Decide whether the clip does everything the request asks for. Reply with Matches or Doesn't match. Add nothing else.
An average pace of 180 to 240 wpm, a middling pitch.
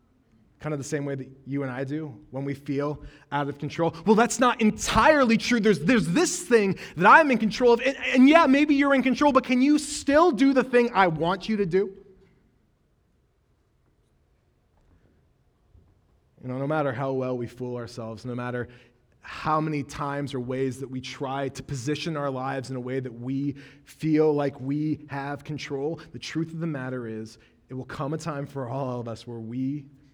Matches